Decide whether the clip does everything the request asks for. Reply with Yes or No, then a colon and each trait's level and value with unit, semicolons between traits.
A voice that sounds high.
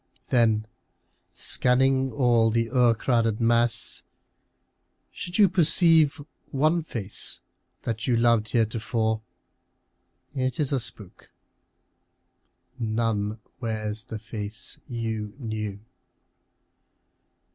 No: low, 115 Hz